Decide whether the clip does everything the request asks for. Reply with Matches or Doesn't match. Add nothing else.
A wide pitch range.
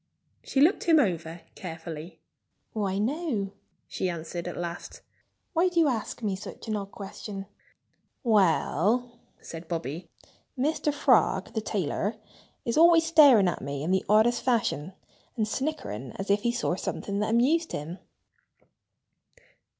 Matches